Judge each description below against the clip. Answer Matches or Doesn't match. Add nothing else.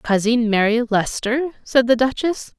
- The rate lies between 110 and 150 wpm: Matches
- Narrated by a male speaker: Doesn't match